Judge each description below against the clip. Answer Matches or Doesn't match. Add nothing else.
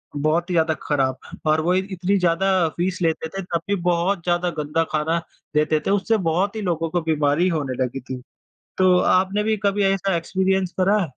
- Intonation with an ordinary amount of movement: Matches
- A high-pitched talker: Doesn't match